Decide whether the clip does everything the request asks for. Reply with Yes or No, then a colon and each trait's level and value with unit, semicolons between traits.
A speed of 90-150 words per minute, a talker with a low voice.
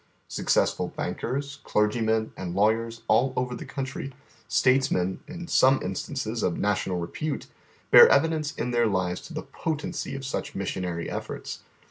Yes: average, 145 wpm; low, 120 Hz